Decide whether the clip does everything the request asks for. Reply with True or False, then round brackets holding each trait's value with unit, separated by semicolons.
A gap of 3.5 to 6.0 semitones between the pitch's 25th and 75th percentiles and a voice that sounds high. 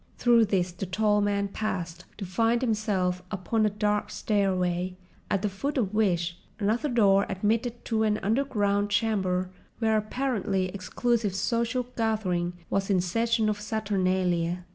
False (3.1 semitones; 205 Hz)